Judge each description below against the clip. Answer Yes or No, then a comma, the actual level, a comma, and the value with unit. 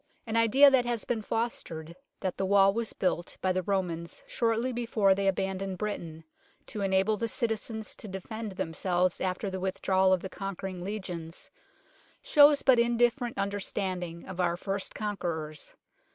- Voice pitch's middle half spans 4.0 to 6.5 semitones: No, average, 3.5 semitones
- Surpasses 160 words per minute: No, average, 155 wpm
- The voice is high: Yes, high, 195 Hz